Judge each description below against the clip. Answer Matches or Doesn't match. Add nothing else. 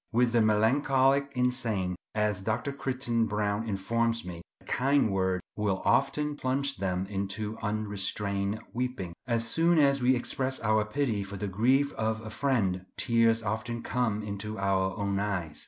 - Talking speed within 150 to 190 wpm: Matches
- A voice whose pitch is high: Doesn't match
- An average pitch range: Matches